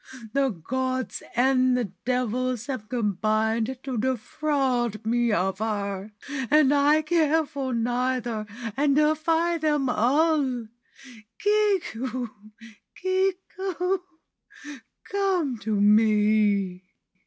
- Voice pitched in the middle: No, very high, 255 Hz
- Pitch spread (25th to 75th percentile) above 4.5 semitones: Yes, wide, 5.5 semitones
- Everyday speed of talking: No, slow, 90 wpm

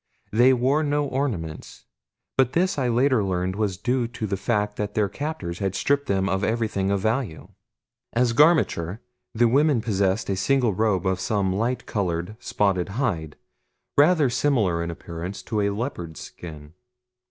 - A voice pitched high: No, low, 105 Hz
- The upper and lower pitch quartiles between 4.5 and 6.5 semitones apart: Yes, average, 5.2 semitones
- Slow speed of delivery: No, average, 160 wpm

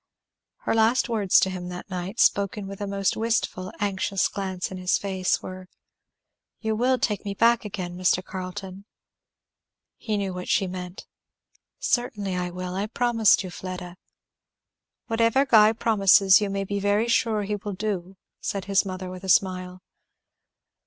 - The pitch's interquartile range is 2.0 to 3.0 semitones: Yes, narrow, 2.5 semitones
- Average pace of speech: Yes, average, 160 wpm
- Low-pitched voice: No, high, 195 Hz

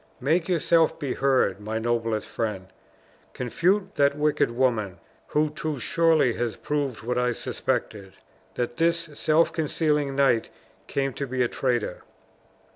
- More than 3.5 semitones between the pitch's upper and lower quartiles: Yes, average, 4.7 semitones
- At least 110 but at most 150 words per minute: Yes, slow, 135 wpm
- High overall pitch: No, low, 135 Hz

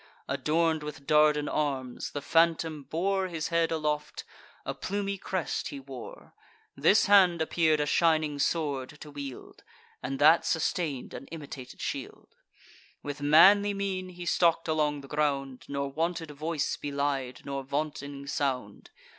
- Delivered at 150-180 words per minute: No, average, 140 wpm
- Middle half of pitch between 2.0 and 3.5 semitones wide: Yes, average, 3.0 semitones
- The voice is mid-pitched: Yes, medium, 150 Hz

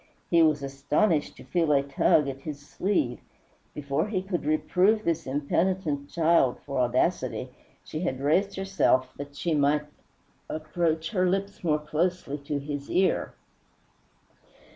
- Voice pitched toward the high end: No, medium, 155 Hz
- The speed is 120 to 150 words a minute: Yes, average, 140 wpm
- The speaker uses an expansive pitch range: No, average, 4.1 semitones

